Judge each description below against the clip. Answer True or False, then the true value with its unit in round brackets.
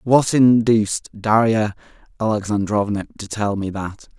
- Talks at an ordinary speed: False (115 wpm)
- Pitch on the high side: False (105 Hz)